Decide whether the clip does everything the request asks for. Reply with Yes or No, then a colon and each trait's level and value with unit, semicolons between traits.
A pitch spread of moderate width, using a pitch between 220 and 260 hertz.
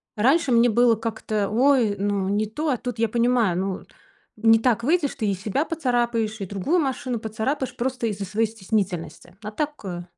Yes: average, 3.6 semitones; high, 225 Hz